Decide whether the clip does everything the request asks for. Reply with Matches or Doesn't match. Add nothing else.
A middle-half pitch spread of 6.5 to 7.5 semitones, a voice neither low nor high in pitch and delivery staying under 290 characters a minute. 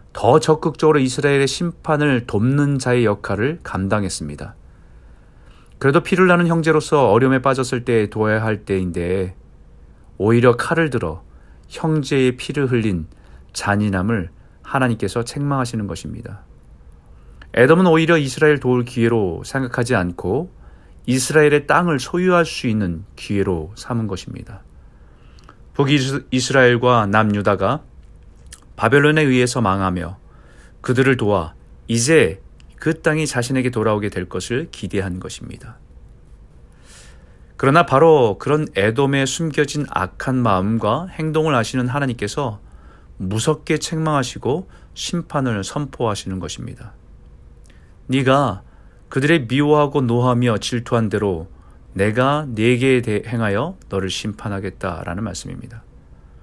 Doesn't match